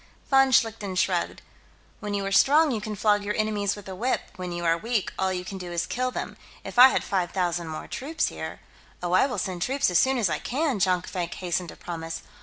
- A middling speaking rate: No, fast, 230 wpm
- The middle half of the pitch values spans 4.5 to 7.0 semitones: Yes, average, 5.1 semitones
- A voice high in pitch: Yes, high, 195 Hz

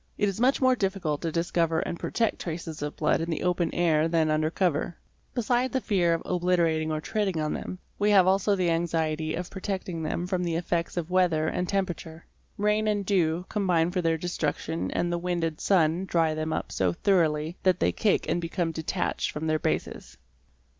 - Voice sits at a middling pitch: Yes, medium, 170 Hz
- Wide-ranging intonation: No, average, 2.8 semitones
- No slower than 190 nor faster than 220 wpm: Yes, average, 200 wpm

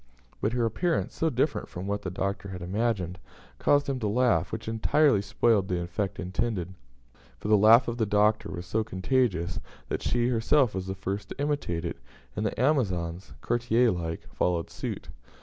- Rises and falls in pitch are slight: No, average, 4.4 semitones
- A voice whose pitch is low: Yes, low, 105 Hz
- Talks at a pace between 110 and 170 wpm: No, average, 180 wpm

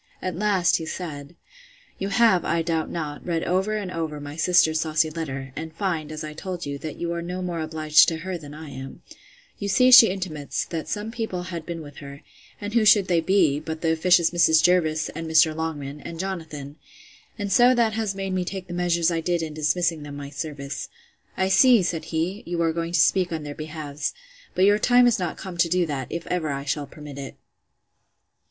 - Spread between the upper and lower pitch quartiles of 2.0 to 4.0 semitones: Yes, average, 3.2 semitones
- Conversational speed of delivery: No, fast, 215 wpm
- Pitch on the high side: No, medium, 165 Hz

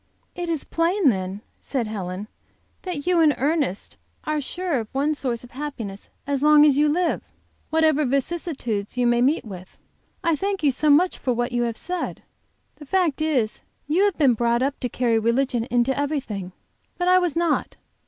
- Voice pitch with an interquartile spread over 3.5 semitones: Yes, average, 5.1 semitones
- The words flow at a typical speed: Yes, average, 185 wpm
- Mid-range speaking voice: No, very high, 280 Hz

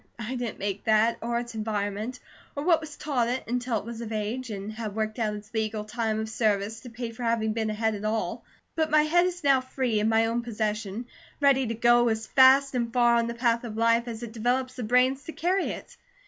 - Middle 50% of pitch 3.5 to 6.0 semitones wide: No, narrow, 2.5 semitones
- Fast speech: Yes, fast, 240 wpm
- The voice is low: No, high, 230 Hz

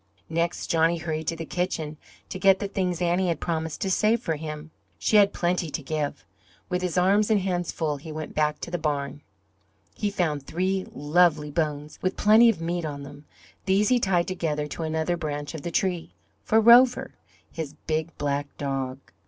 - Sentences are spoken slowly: No, average, 190 wpm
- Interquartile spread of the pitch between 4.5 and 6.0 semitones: No, average, 3.6 semitones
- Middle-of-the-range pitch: Yes, medium, 165 Hz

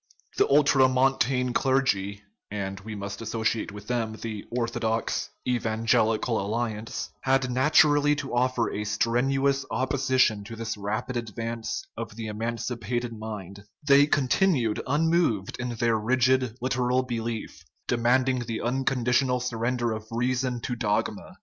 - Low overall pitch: Yes, low, 120 Hz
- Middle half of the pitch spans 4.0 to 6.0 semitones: No, average, 2.9 semitones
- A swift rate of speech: No, slow, 135 wpm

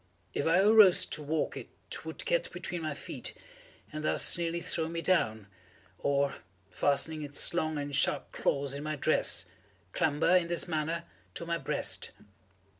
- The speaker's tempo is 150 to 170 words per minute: Yes, average, 160 wpm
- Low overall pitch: No, medium, 160 Hz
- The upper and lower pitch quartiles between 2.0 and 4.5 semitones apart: Yes, average, 3.0 semitones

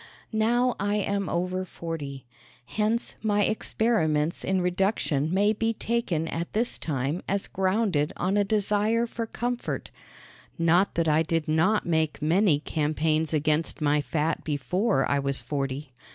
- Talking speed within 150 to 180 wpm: No, average, 140 wpm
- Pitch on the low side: No, medium, 175 Hz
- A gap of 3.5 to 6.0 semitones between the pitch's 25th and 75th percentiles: Yes, average, 5.3 semitones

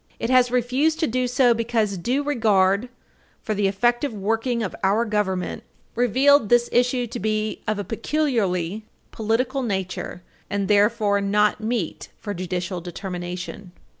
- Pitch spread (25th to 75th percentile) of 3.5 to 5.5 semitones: Yes, average, 3.8 semitones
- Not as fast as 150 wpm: Yes, average, 140 wpm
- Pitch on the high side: Yes, high, 215 Hz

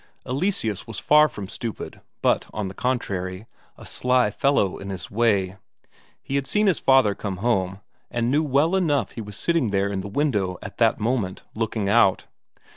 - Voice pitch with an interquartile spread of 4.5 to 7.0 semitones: Yes, average, 5.3 semitones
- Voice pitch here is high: No, low, 115 Hz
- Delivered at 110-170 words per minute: No, average, 180 wpm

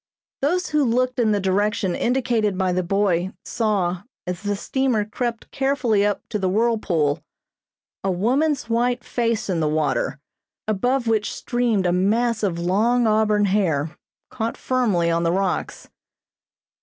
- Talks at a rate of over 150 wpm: No, average, 145 wpm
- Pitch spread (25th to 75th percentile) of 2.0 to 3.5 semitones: No, average, 4.5 semitones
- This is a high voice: Yes, high, 210 Hz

